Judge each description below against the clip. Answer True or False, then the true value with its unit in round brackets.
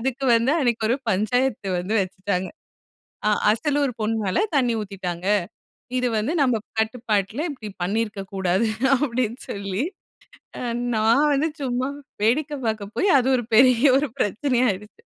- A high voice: True (230 Hz)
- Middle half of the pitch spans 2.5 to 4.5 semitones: True (4.1 semitones)